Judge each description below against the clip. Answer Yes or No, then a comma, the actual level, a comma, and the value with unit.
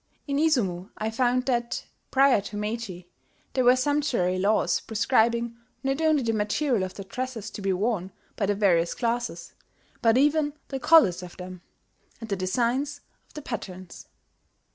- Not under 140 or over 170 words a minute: Yes, average, 160 wpm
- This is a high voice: Yes, high, 230 Hz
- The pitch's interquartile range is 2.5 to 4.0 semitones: No, average, 5.1 semitones